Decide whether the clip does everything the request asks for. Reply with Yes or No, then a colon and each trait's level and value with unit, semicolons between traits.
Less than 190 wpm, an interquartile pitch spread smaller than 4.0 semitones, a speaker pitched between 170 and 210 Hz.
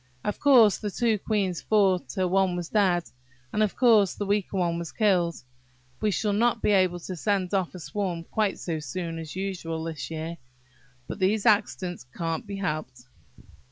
Yes: average, 180 wpm; average, 3.6 semitones; medium, 185 Hz